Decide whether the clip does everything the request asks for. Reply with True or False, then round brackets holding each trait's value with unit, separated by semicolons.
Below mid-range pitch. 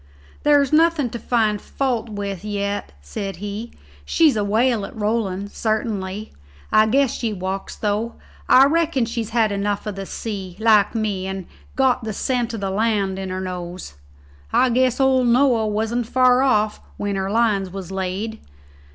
False (215 Hz)